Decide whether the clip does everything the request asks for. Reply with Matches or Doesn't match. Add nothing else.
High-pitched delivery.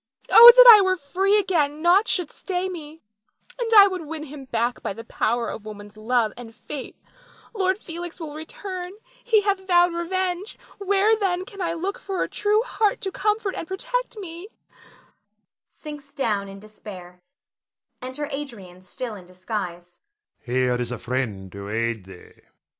Matches